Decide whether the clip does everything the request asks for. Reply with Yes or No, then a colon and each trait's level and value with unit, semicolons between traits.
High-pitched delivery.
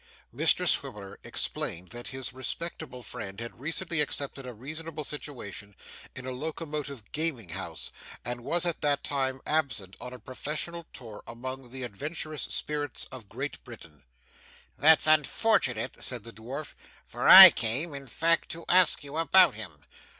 No: low, 135 Hz